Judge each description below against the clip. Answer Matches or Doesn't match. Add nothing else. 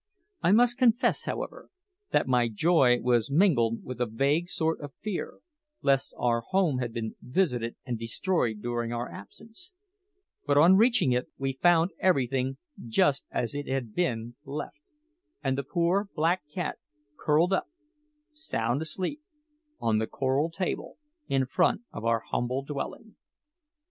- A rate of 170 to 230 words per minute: Doesn't match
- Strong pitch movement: Matches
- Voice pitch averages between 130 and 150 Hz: Matches